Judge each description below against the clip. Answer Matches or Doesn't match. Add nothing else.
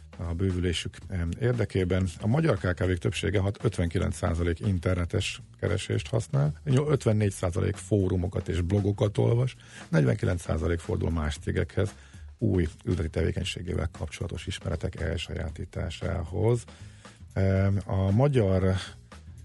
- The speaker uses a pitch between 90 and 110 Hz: Matches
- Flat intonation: Doesn't match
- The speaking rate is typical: Doesn't match